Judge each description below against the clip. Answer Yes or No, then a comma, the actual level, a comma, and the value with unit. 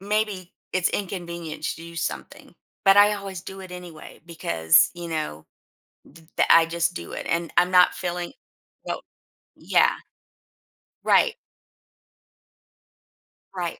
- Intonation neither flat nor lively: No, narrow, 2.3 semitones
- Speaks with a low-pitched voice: No, medium, 175 Hz